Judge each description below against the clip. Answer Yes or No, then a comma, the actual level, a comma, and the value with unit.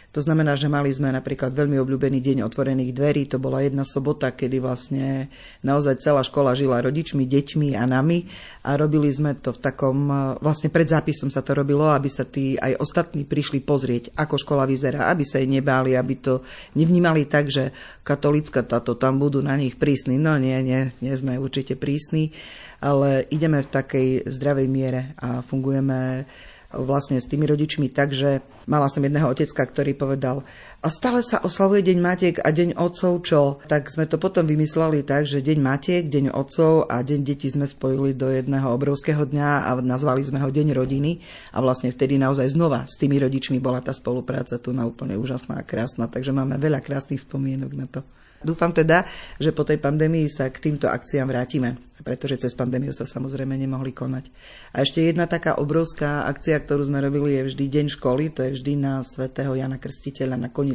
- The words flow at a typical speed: No, fast, 185 wpm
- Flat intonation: Yes, narrow, 2.1 semitones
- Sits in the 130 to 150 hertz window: Yes, medium, 140 Hz